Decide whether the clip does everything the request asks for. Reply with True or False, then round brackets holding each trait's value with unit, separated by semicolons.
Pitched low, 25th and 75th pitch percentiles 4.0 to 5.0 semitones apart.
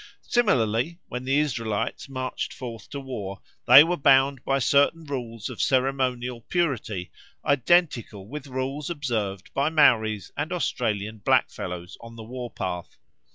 True (125 Hz; 4.3 semitones)